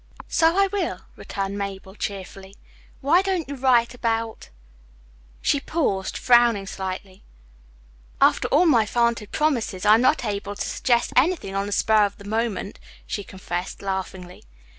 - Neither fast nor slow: Yes, average, 145 wpm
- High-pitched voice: Yes, high, 215 Hz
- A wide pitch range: No, average, 4.6 semitones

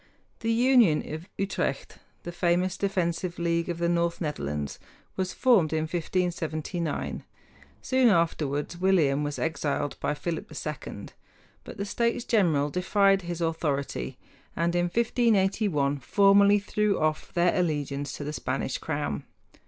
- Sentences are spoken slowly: Yes, slow, 130 wpm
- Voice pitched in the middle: Yes, medium, 170 Hz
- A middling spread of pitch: Yes, average, 4.4 semitones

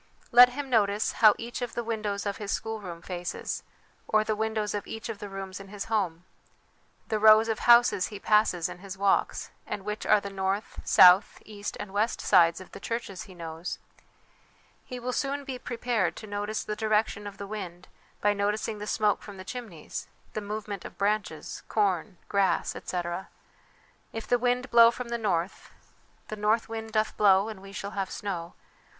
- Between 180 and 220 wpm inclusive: Yes, average, 185 wpm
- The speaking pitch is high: Yes, high, 210 Hz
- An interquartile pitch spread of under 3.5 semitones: Yes, narrow, 2.4 semitones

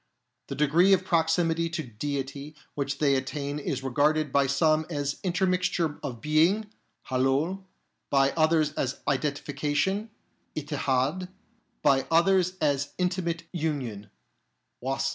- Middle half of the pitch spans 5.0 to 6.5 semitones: No, average, 3.4 semitones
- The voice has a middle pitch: Yes, medium, 150 Hz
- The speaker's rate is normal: No, slow, 115 wpm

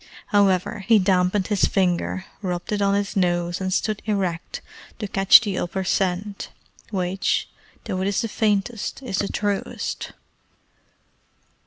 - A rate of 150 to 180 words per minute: No, average, 140 wpm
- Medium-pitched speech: No, high, 195 Hz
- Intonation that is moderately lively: No, narrow, 1.9 semitones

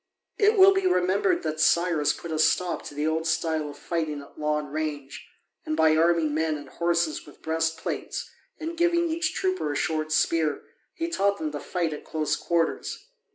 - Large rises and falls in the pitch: No, average, 3.5 semitones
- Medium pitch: Yes, medium, 160 Hz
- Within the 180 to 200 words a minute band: Yes, average, 185 wpm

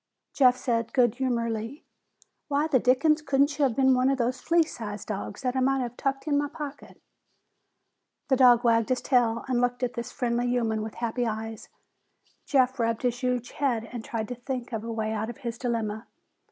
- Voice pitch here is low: No, high, 245 Hz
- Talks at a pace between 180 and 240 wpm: Yes, average, 195 wpm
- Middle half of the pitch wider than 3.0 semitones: No, narrow, 2.5 semitones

